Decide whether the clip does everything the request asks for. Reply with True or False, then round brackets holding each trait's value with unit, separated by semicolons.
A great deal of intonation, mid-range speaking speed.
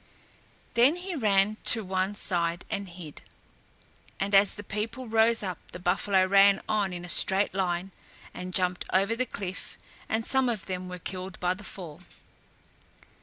False (2.8 semitones; 165 wpm)